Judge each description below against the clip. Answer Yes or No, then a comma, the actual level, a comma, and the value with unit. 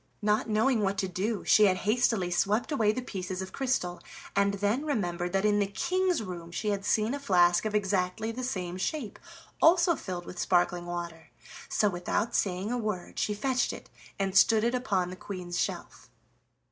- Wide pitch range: No, average, 3.8 semitones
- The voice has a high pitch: Yes, high, 200 Hz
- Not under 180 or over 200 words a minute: Yes, average, 185 wpm